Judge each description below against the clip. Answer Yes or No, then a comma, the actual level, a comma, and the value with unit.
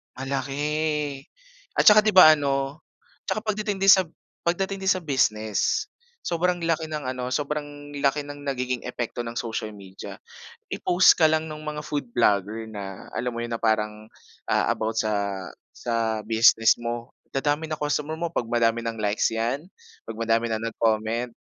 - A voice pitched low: Yes, low, 130 Hz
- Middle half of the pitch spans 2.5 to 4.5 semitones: No, average, 5.3 semitones